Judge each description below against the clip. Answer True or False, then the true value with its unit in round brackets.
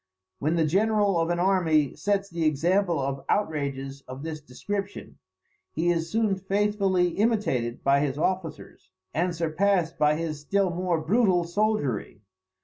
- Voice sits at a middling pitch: True (170 Hz)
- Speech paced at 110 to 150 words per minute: True (140 wpm)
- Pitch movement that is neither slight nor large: True (4.7 semitones)